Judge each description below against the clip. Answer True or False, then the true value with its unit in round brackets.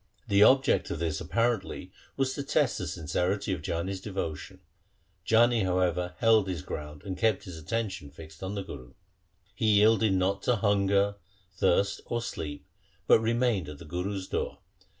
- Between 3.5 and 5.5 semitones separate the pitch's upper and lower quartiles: True (4.1 semitones)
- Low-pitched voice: True (95 Hz)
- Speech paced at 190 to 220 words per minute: False (160 wpm)